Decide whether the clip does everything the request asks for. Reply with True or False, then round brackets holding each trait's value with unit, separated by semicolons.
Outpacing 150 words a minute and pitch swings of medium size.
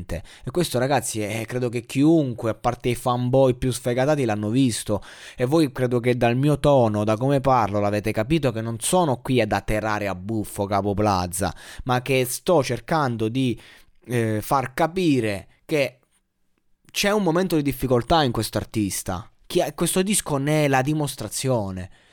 True (165 wpm; 4.5 semitones)